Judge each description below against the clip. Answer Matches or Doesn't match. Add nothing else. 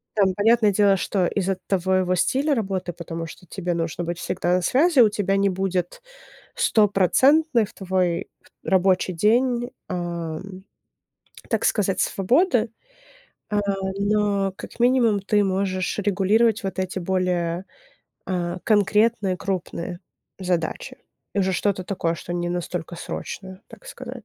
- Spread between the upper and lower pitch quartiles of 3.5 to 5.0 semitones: Doesn't match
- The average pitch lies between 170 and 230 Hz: Matches